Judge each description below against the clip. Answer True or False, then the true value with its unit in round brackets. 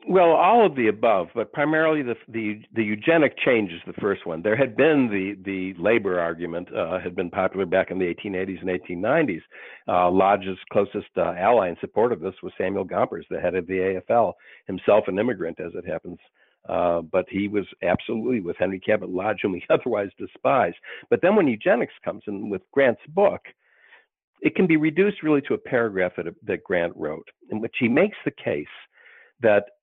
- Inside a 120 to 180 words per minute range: False (195 wpm)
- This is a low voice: True (100 Hz)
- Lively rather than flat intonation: True (7.7 semitones)